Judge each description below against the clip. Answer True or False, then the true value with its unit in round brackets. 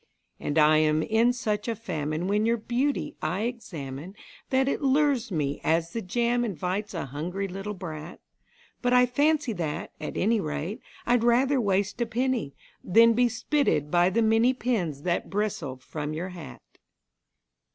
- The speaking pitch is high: True (205 Hz)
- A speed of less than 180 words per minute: True (160 wpm)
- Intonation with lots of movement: True (6.9 semitones)